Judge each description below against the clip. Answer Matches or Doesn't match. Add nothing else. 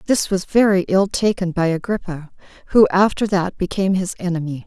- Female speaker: Matches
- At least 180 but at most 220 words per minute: Doesn't match